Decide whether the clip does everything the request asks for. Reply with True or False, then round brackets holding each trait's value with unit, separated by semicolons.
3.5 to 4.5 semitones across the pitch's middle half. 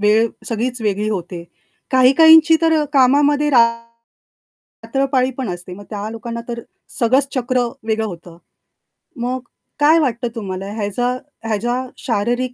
True (3.9 semitones)